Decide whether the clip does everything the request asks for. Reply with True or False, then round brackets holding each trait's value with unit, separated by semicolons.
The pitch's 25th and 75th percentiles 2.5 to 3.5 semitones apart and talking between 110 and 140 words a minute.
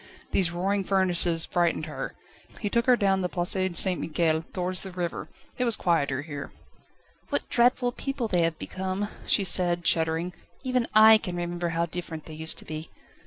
False (3.1 semitones; 175 wpm)